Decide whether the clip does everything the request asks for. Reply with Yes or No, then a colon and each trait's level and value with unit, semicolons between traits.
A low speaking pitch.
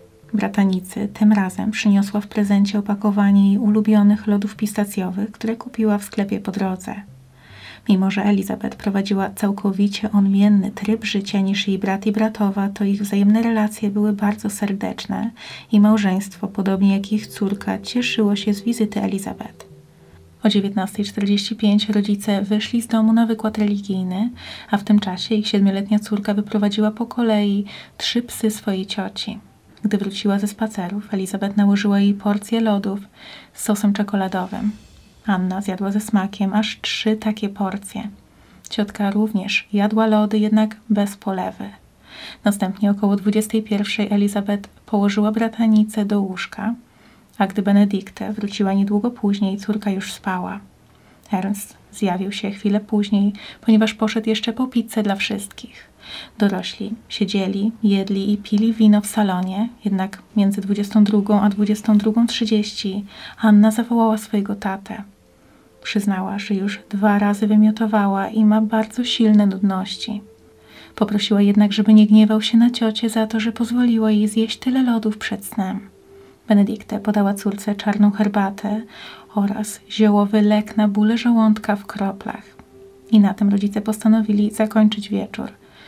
No: high, 210 Hz